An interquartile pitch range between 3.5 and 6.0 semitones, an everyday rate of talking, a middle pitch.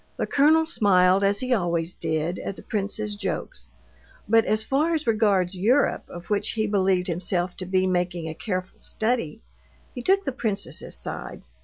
No: average, 3.9 semitones; average, 170 wpm; high, 200 Hz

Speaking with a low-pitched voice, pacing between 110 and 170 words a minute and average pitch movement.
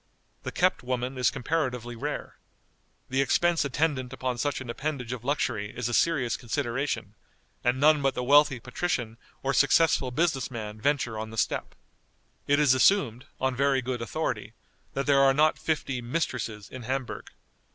Yes: low, 130 Hz; average, 160 wpm; average, 3.0 semitones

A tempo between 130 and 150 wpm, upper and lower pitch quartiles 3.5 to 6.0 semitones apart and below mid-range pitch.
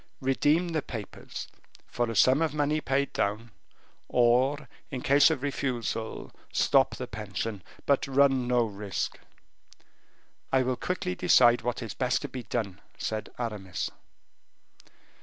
Yes: slow, 135 wpm; average, 3.9 semitones; low, 125 Hz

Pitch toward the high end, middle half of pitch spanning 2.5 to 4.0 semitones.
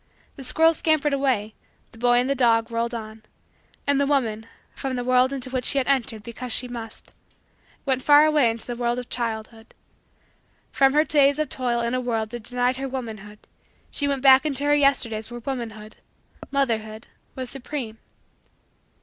Yes: very high, 250 Hz; average, 3.3 semitones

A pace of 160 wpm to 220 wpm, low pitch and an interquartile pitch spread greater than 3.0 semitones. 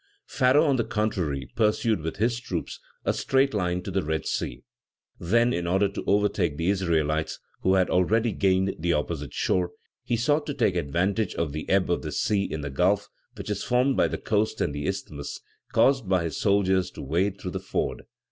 Yes: average, 200 wpm; very low, 95 Hz; average, 4.4 semitones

